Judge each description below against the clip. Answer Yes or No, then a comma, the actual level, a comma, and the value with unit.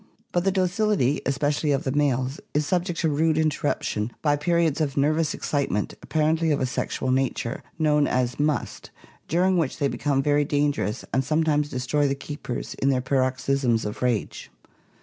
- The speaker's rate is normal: Yes, average, 170 wpm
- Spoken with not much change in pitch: No, average, 3.0 semitones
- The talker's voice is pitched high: No, medium, 145 Hz